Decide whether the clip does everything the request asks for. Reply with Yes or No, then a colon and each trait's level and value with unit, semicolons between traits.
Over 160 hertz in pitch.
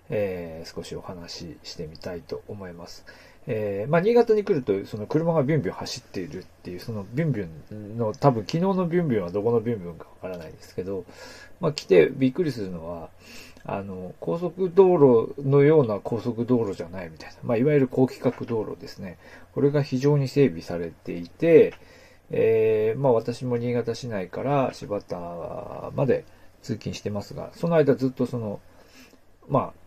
No: low, 120 Hz